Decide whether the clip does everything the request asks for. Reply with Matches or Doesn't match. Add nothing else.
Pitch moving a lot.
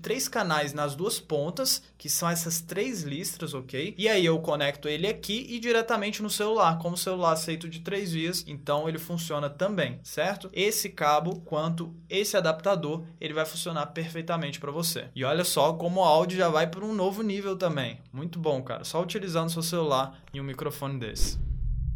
Doesn't match